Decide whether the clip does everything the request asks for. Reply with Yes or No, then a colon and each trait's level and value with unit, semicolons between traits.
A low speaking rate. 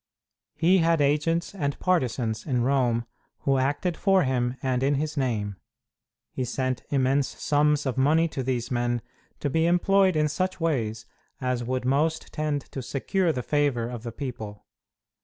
No: average, 160 wpm